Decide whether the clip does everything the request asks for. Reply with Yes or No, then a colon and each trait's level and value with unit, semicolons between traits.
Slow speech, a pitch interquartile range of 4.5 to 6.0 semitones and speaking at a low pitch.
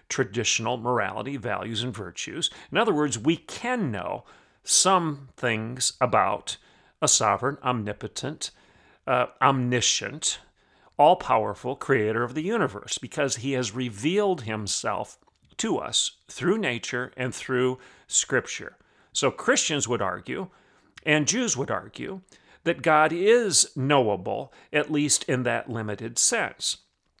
Yes: slow, 120 wpm; average, 4.8 semitones; low, 125 Hz